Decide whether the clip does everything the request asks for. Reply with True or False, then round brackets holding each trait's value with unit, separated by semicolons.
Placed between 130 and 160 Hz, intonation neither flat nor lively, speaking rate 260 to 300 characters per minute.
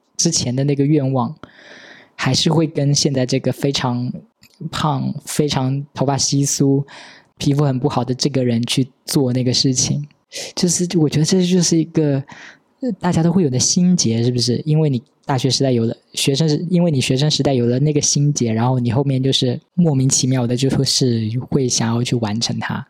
True (140 Hz; 3.3 semitones; 280 characters per minute)